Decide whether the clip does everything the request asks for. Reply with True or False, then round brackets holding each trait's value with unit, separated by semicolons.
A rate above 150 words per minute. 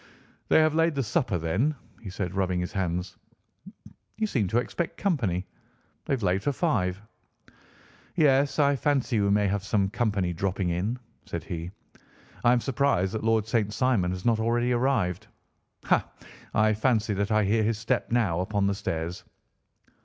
True (170 wpm)